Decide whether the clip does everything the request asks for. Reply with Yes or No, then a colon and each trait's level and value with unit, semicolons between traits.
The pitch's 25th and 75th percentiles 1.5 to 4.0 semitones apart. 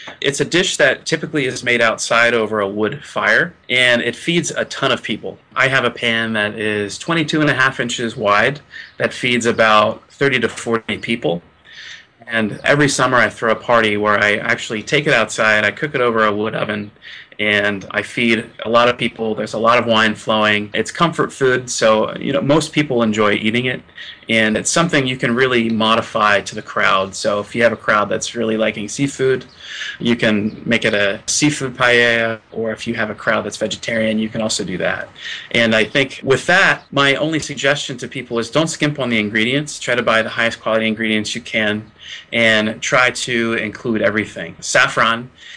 Yes: average, 3.2 semitones